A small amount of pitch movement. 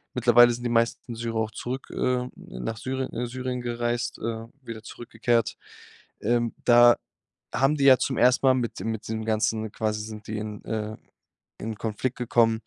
Yes: narrow, 1.8 semitones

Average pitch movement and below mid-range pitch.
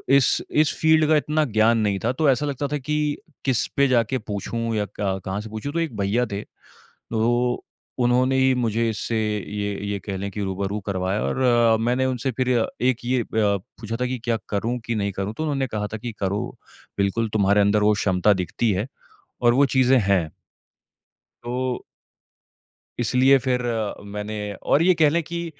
Yes: average, 4.0 semitones; low, 115 Hz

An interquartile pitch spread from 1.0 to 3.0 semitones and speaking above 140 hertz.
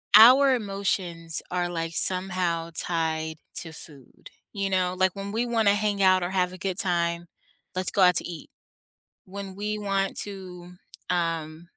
Yes: average, 2.7 semitones; medium, 185 Hz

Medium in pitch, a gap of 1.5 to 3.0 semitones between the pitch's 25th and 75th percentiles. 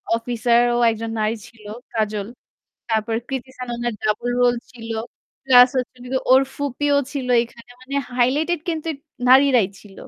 No: high, 245 Hz; narrow, 2.6 semitones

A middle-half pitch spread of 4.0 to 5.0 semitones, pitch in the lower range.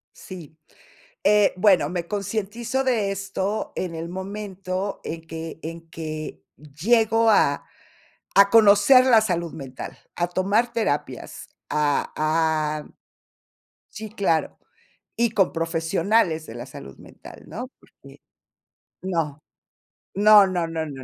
No: average, 4.6 semitones; medium, 185 Hz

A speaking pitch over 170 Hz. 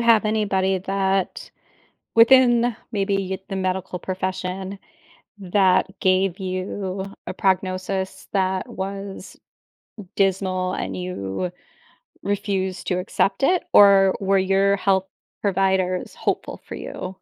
Yes: high, 190 Hz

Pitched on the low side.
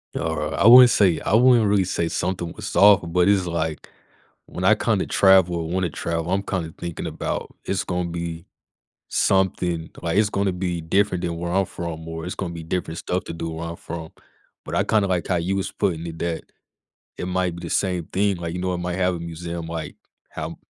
Yes: very low, 90 Hz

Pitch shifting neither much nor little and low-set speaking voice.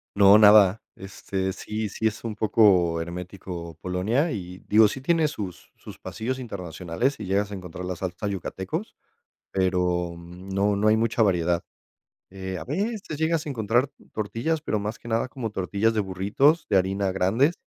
Yes: average, 3.7 semitones; low, 100 Hz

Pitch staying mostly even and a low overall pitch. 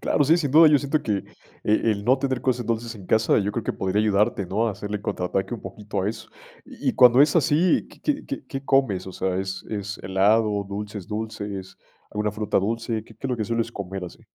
No: average, 3.5 semitones; low, 110 Hz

